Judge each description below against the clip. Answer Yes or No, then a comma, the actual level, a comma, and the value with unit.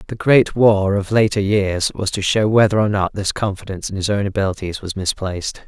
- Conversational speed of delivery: No, fast, 210 wpm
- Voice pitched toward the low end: Yes, low, 100 Hz